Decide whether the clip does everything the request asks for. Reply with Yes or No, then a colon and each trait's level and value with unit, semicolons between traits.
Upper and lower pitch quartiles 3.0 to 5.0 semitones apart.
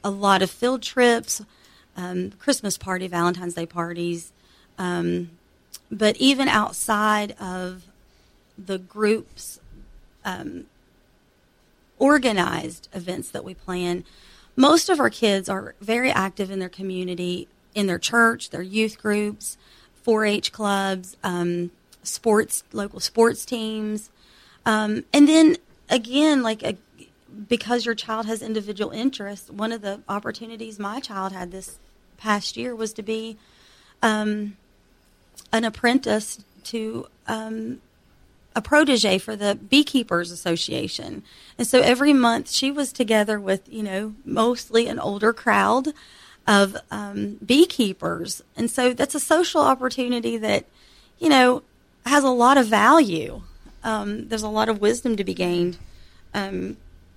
Yes: average, 4.2 semitones